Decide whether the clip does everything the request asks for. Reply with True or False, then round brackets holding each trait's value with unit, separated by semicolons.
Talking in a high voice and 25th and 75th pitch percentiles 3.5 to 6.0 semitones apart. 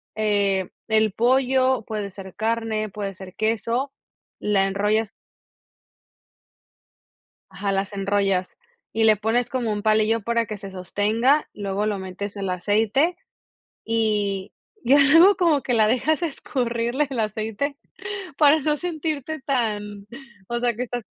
True (220 Hz; 4.0 semitones)